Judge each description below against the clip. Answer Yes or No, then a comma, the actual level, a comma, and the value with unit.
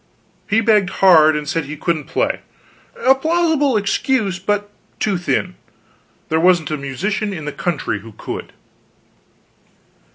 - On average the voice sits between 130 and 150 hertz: No, medium, 185 Hz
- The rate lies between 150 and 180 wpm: No, slow, 135 wpm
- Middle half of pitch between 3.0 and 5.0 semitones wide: No, wide, 5.4 semitones